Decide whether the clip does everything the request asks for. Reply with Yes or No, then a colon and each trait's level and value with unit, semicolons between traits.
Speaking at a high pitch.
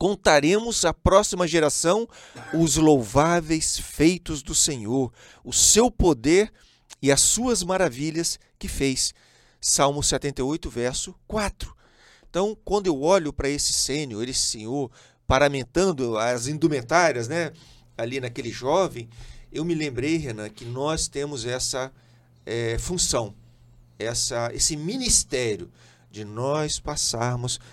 No: medium, 145 Hz